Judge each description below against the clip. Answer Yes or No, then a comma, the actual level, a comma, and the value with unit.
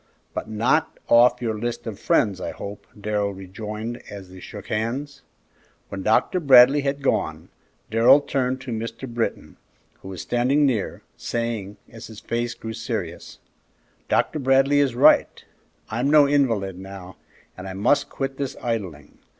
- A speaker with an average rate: Yes, average, 150 wpm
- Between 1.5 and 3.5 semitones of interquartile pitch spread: No, average, 4.8 semitones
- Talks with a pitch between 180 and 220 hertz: No, low, 115 Hz